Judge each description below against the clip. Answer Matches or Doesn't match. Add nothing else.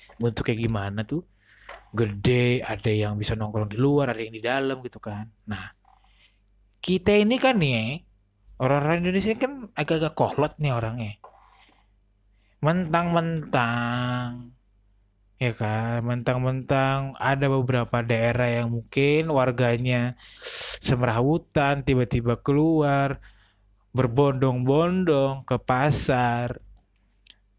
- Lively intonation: Doesn't match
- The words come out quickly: Doesn't match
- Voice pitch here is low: Matches